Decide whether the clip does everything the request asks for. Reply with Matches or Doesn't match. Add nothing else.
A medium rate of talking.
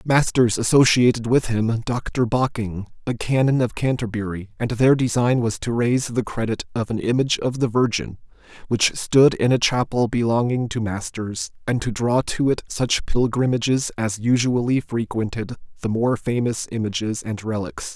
Matches